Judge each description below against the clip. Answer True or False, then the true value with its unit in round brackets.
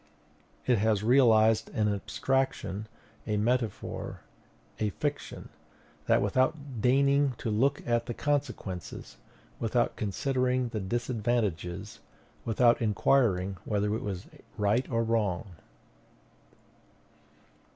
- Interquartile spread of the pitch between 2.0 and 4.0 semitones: True (3.5 semitones)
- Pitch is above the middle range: False (115 Hz)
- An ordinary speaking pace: False (100 wpm)